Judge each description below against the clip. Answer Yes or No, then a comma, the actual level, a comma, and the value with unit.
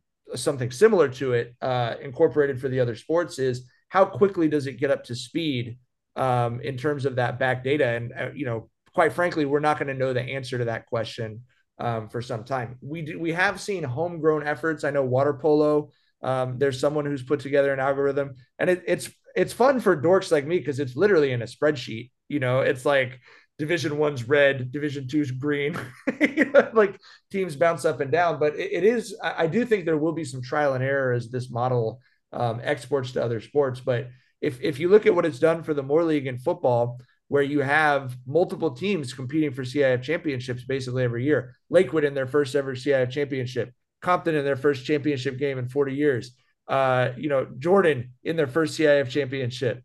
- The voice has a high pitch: No, medium, 140 Hz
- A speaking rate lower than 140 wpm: No, fast, 205 wpm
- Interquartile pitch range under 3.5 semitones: No, average, 3.8 semitones